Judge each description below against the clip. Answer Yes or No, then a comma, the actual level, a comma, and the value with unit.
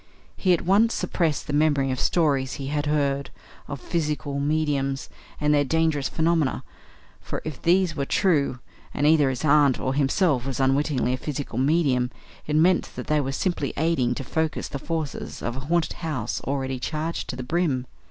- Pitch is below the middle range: No, medium, 145 Hz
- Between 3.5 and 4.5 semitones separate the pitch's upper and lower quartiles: No, average, 3.0 semitones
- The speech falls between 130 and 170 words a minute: No, average, 180 wpm